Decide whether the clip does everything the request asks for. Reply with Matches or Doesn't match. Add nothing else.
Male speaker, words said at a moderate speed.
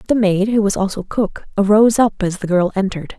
Doesn't match